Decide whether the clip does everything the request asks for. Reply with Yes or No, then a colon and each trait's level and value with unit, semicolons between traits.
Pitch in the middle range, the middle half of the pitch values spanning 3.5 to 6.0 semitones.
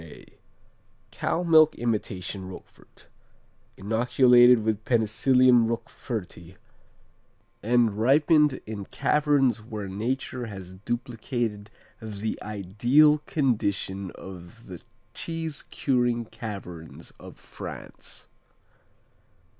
No: low, 115 Hz; average, 4.1 semitones